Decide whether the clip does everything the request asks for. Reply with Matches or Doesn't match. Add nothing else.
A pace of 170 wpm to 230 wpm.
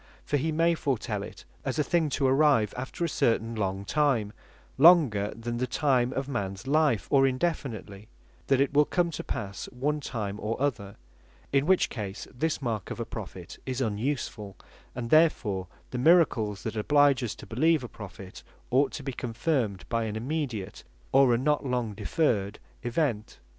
Matches